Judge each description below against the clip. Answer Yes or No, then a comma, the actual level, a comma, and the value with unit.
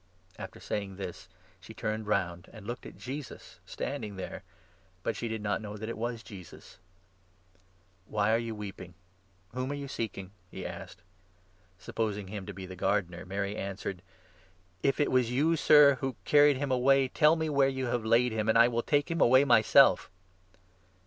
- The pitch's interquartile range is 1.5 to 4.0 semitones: No, average, 4.8 semitones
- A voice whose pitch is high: No, low, 110 Hz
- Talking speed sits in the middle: Yes, average, 190 wpm